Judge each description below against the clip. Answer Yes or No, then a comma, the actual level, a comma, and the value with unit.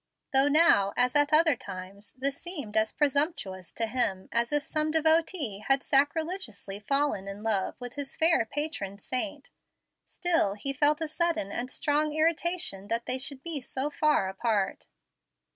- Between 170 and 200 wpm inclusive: No, average, 160 wpm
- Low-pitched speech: No, very high, 275 Hz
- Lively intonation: Yes, wide, 6.5 semitones